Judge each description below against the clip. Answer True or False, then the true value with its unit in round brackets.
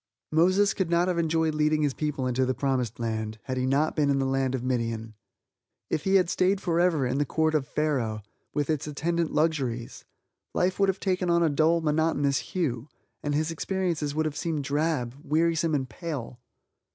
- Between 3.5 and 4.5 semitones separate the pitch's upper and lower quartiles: True (4.0 semitones)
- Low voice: False (150 Hz)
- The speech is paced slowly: False (190 wpm)